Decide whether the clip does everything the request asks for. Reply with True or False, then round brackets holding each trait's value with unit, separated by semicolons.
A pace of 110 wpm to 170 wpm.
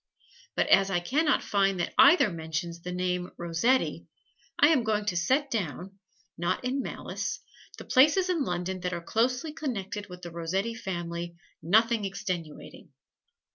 True (155 wpm)